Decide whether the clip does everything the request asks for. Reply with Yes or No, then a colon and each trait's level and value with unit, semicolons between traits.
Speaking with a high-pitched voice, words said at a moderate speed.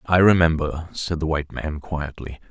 No: very low, 80 Hz; average, 170 wpm